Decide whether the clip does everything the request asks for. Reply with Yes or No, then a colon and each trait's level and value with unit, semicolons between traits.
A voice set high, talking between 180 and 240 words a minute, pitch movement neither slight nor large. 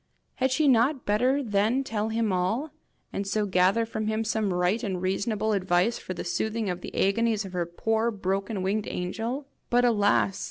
Yes: high, 215 Hz; average, 185 wpm; average, 3.3 semitones